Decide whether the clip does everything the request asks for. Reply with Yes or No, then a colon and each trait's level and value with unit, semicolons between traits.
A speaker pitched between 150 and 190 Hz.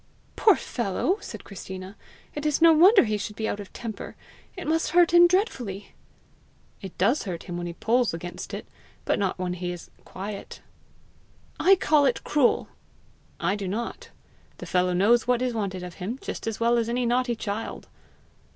No: high, 225 Hz